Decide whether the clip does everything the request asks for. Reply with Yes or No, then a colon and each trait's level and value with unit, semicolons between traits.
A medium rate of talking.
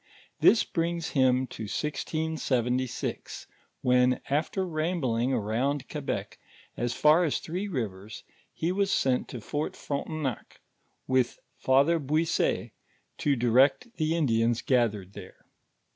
No: slow, 115 wpm